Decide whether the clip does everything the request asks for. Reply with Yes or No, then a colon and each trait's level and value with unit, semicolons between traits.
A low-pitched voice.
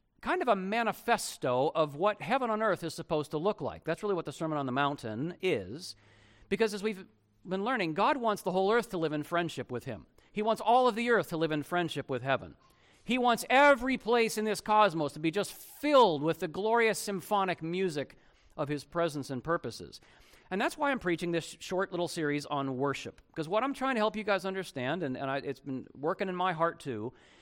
No: medium, 175 Hz